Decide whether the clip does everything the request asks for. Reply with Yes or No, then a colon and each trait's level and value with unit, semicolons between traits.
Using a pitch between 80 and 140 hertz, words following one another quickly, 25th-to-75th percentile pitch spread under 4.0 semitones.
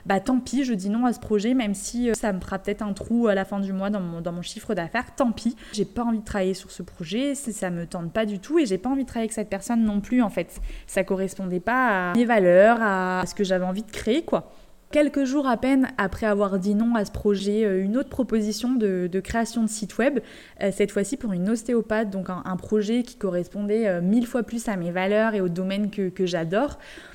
No: high, 210 Hz; fast, 255 wpm; average, 3.4 semitones